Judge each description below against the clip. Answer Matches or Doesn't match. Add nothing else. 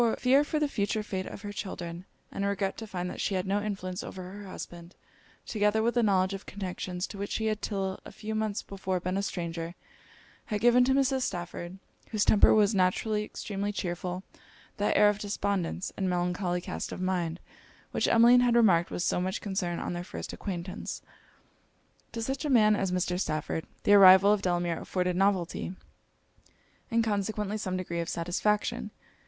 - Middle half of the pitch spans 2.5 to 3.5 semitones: Matches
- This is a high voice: Matches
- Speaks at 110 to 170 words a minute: Doesn't match